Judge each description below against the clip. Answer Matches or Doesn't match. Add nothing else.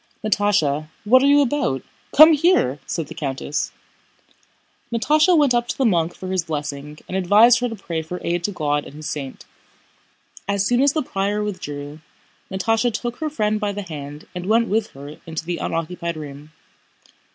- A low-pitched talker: Doesn't match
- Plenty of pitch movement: Matches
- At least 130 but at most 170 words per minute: Doesn't match